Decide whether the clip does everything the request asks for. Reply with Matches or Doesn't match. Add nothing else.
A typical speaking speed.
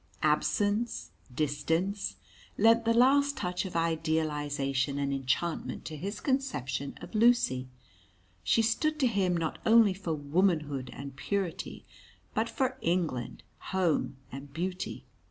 Doesn't match